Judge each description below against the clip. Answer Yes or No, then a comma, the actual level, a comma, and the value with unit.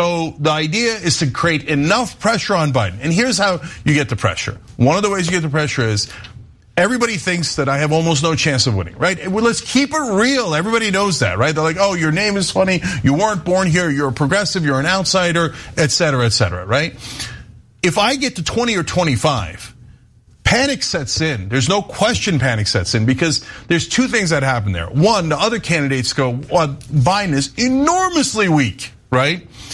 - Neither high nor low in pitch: Yes, medium, 160 Hz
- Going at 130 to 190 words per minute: No, average, 200 wpm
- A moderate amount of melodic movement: No, wide, 6.5 semitones